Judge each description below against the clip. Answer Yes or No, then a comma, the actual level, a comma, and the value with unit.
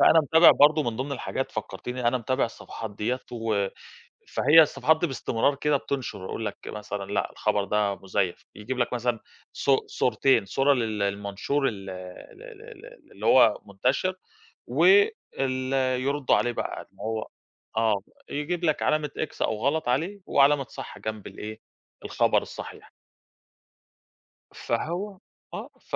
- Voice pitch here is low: Yes, low, 130 Hz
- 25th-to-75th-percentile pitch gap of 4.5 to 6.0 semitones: Yes, wide, 5.6 semitones